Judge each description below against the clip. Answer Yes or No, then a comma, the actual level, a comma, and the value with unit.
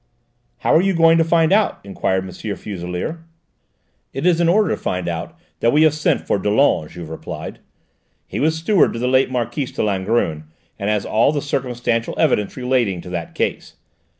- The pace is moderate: Yes, average, 190 wpm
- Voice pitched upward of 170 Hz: No, low, 120 Hz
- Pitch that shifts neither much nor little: No, wide, 8.6 semitones